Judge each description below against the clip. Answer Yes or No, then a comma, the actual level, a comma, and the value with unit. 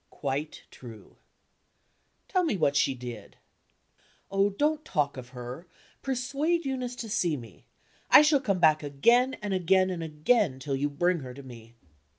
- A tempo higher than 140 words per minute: Yes, average, 160 wpm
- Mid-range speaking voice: Yes, medium, 165 Hz